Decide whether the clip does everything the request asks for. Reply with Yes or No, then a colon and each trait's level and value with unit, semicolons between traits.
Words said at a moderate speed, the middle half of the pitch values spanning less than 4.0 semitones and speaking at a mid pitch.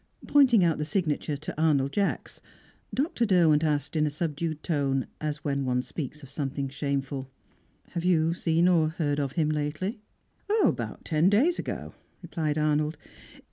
Yes: average, 155 wpm; average, 2.8 semitones; medium, 155 Hz